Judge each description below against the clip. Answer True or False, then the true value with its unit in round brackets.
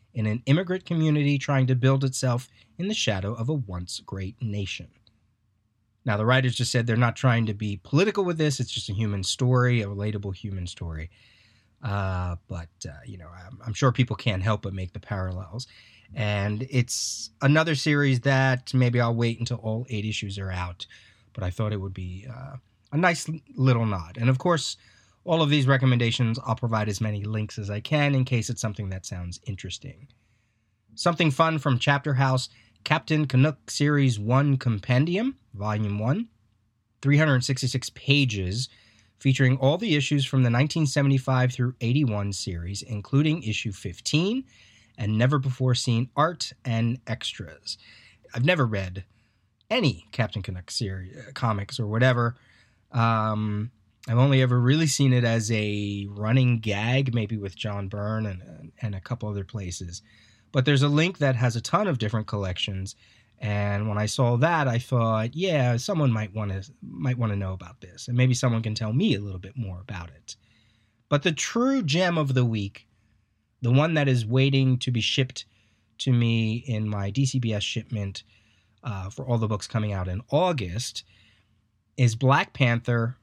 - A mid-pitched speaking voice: False (115 Hz)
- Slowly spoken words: False (175 wpm)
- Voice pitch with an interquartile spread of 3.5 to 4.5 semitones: True (3.9 semitones)